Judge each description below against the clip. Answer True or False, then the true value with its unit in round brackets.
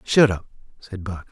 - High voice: False (100 Hz)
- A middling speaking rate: True (185 wpm)